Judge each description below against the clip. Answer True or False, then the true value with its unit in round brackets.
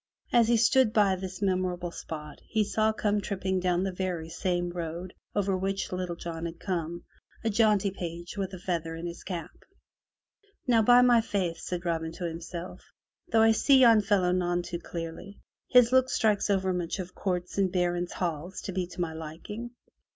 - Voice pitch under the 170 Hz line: False (185 Hz)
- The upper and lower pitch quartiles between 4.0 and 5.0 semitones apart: False (3.0 semitones)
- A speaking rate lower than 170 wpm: False (180 wpm)